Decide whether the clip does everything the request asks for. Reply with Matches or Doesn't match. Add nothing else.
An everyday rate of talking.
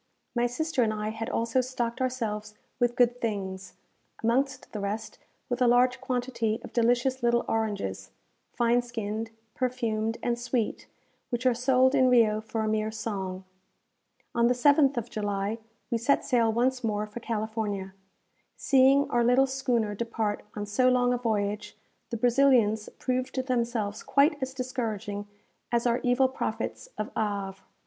Matches